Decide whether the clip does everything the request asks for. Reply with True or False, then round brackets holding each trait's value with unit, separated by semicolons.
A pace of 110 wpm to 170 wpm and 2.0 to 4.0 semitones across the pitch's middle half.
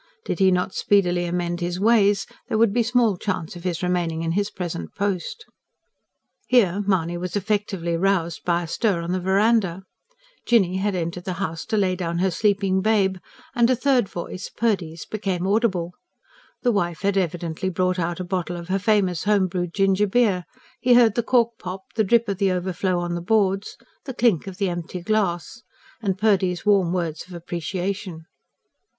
False (180 wpm; 2.9 semitones)